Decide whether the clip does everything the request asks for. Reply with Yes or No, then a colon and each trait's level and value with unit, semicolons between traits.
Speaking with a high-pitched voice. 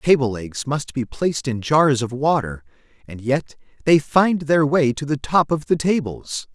No: medium, 140 Hz